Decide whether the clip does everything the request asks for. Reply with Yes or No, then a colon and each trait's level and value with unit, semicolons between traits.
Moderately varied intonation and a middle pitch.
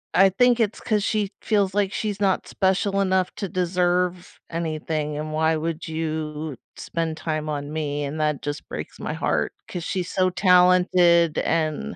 Yes: average, 3.3 semitones; medium, 170 Hz